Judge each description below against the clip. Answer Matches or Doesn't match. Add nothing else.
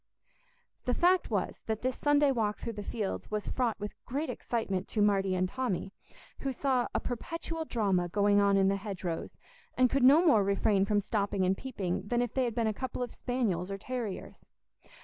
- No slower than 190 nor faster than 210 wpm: Matches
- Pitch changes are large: Doesn't match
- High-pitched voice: Matches